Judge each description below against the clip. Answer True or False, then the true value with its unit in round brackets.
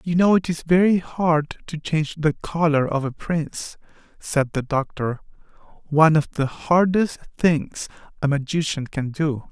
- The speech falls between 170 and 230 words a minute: False (150 wpm)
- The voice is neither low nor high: True (155 Hz)